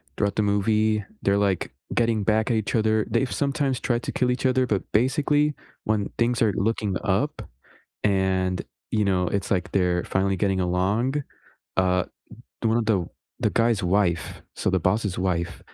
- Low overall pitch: Yes, low, 105 Hz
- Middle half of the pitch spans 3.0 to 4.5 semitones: Yes, average, 3.6 semitones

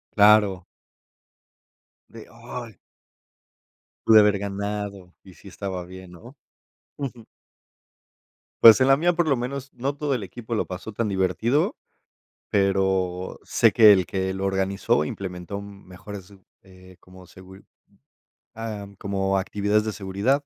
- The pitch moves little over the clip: No, average, 3.1 semitones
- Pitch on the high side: No, low, 100 Hz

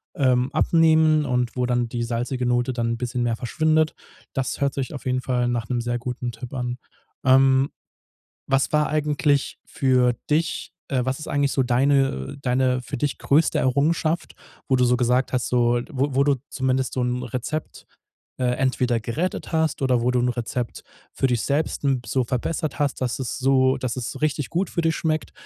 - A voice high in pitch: No, low, 130 Hz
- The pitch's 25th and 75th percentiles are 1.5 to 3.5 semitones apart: Yes, narrow, 2.6 semitones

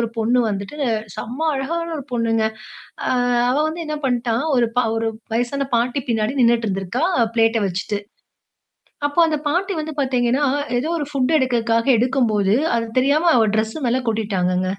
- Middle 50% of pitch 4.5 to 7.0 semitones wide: No, average, 3.7 semitones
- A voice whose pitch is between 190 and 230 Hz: No, high, 240 Hz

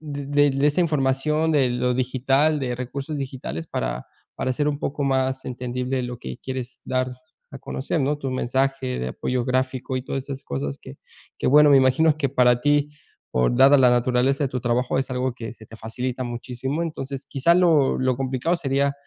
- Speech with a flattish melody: Yes, narrow, 2.0 semitones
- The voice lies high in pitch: No, low, 130 Hz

